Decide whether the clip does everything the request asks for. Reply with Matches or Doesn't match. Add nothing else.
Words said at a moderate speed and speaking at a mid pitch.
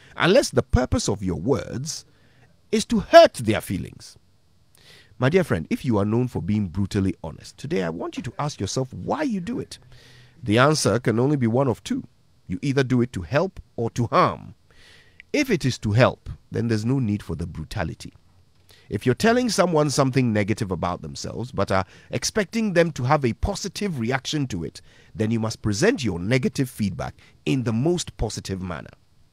Doesn't match